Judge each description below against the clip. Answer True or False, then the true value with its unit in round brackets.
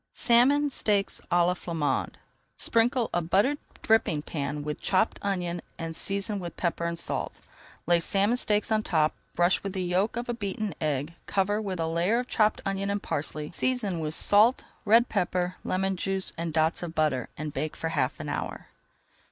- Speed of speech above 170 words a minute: True (180 wpm)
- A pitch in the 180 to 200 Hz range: True (185 Hz)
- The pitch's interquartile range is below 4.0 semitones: False (4.3 semitones)